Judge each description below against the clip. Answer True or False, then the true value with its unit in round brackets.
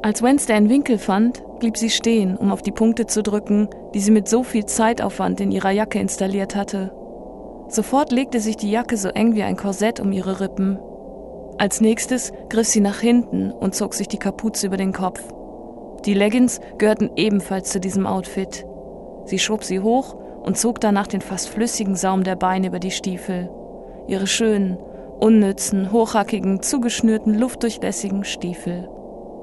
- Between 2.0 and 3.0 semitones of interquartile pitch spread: True (2.6 semitones)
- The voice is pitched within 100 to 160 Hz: False (205 Hz)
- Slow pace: False (165 wpm)